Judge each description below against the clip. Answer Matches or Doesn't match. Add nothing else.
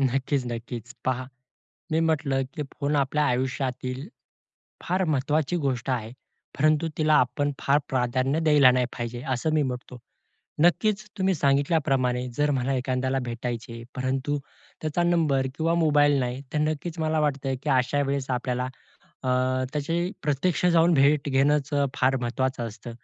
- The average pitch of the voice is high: Doesn't match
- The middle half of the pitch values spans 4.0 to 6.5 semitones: Doesn't match